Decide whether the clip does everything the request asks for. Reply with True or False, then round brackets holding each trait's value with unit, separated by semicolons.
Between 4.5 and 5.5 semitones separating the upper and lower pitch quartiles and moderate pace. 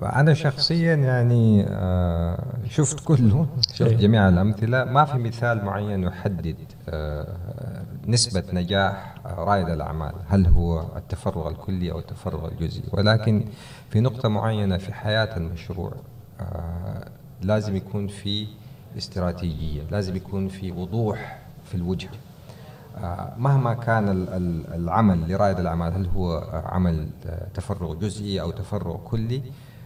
True (4.8 semitones; 110 wpm)